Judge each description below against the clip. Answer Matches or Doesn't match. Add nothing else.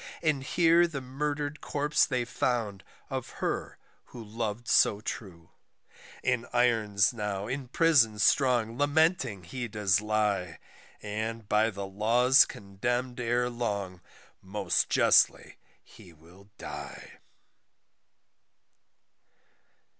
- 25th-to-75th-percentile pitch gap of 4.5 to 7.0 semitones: Doesn't match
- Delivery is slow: Matches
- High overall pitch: Doesn't match